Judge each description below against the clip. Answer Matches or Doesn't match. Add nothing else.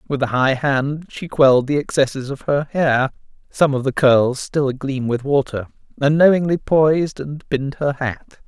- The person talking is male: Matches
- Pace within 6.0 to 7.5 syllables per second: Doesn't match